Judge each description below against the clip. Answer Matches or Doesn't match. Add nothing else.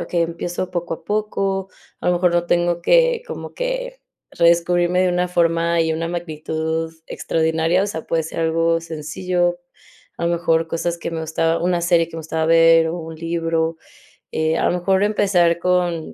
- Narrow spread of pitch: Matches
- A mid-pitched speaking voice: Matches